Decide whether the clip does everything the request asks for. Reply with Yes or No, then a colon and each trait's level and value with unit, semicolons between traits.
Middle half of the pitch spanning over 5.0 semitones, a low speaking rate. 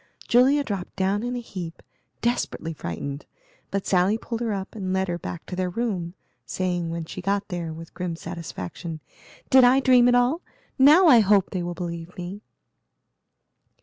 No: wide, 5.5 semitones; average, 175 wpm